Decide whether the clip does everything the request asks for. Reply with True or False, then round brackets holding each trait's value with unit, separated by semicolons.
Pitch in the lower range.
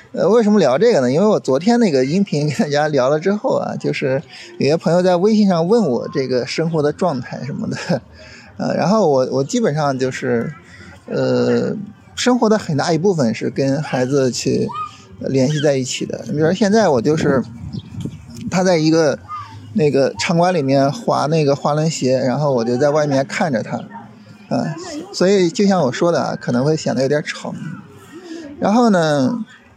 False (160 Hz)